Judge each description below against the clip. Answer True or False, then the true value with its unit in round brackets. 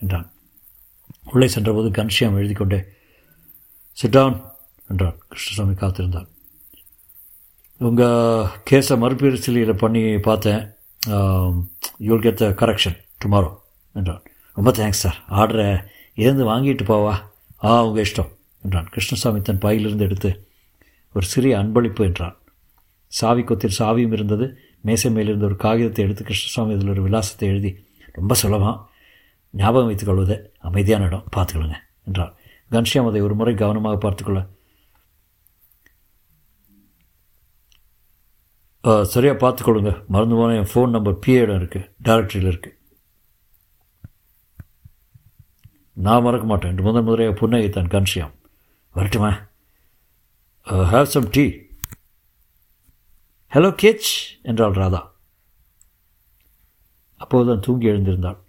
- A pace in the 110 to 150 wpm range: False (100 wpm)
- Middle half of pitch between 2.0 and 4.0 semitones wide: True (3.4 semitones)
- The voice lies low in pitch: True (100 Hz)